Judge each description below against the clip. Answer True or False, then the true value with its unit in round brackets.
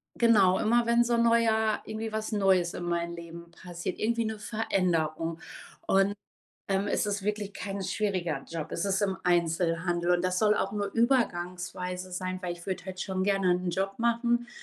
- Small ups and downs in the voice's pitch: False (3.5 semitones)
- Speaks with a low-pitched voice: False (190 Hz)